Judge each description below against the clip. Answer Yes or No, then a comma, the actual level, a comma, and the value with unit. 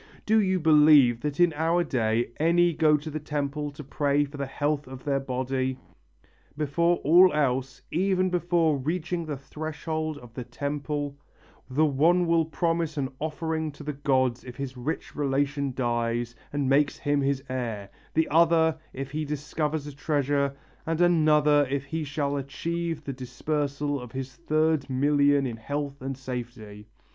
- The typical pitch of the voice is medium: Yes, medium, 145 Hz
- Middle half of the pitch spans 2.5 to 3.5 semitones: Yes, average, 2.8 semitones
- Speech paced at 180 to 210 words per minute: No, average, 160 wpm